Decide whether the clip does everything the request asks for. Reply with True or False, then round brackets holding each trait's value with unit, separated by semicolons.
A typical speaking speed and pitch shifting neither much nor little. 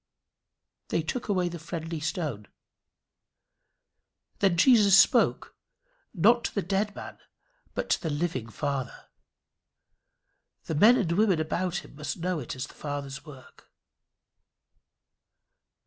False (120 wpm; 4.7 semitones)